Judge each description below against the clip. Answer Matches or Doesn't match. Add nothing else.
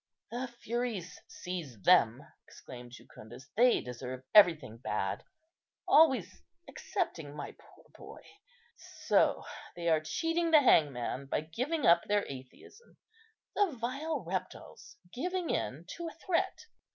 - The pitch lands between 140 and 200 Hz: Matches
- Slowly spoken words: Matches